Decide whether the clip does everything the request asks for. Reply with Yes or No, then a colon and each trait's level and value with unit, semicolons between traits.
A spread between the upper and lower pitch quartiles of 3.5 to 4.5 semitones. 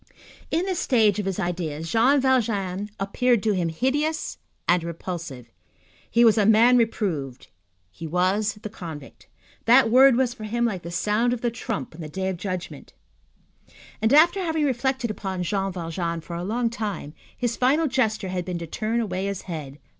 No: wide, 5.4 semitones